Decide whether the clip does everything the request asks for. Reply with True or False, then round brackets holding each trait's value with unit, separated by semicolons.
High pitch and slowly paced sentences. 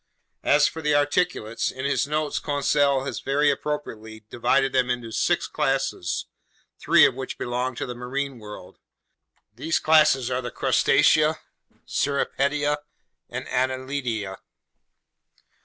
False (135 Hz; 125 wpm)